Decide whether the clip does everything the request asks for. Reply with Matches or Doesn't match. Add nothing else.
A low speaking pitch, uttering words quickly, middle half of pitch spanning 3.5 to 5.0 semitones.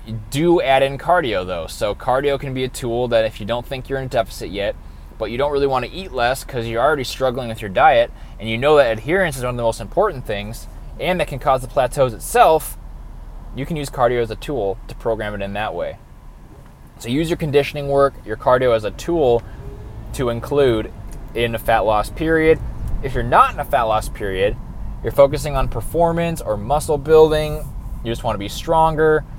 Matches